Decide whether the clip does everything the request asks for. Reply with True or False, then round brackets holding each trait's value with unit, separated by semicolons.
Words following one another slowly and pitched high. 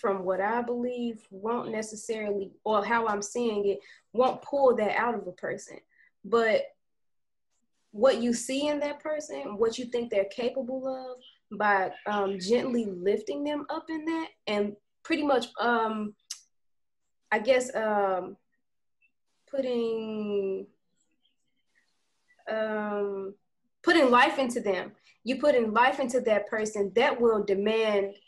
True (130 wpm; 230 Hz)